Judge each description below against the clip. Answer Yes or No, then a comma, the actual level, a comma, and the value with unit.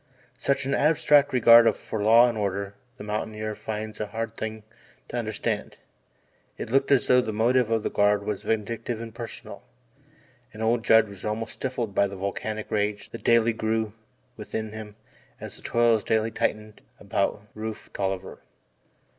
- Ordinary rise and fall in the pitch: No, narrow, 1.7 semitones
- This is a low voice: Yes, low, 110 Hz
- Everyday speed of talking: Yes, average, 165 wpm